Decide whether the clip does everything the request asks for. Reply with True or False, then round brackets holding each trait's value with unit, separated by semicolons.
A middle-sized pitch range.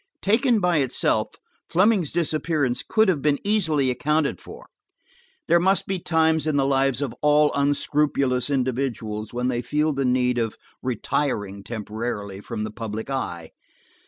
True (4.6 semitones)